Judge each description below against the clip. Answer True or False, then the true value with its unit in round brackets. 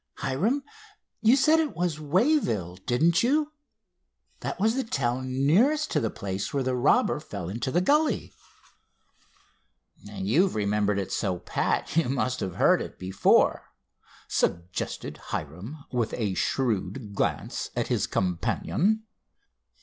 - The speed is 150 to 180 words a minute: False (135 wpm)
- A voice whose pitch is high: False (135 Hz)